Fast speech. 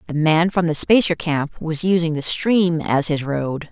Yes: fast, 210 wpm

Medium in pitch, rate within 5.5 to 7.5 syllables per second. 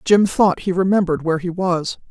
Yes: medium, 180 Hz; 5.7 syllables/s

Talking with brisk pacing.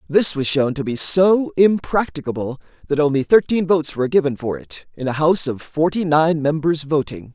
No: average, 190 wpm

